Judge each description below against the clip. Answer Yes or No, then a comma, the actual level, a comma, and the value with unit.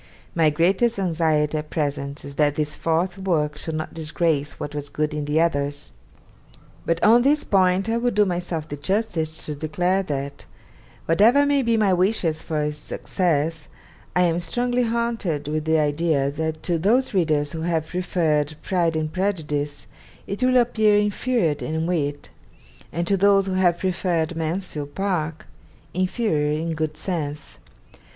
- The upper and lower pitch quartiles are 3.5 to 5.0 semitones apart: Yes, average, 4.1 semitones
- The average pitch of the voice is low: No, medium, 165 Hz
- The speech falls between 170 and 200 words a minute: No, average, 160 wpm